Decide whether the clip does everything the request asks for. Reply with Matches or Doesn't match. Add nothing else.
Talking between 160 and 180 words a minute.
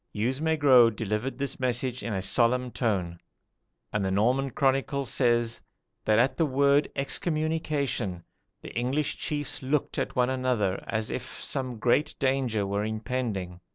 Doesn't match